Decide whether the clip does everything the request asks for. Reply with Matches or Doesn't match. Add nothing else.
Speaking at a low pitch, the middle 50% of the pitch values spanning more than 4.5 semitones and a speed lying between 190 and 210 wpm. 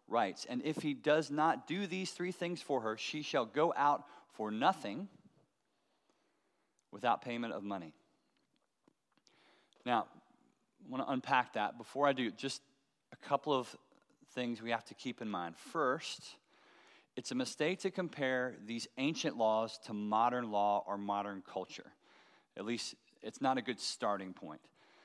Doesn't match